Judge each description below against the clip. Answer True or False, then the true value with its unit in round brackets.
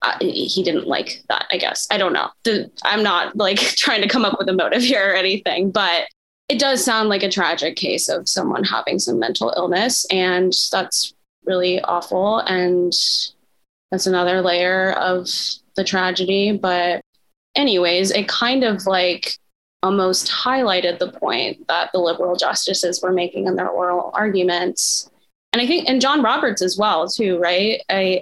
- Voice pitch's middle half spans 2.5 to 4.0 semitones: True (2.8 semitones)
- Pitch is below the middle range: False (185 Hz)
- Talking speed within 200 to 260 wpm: False (170 wpm)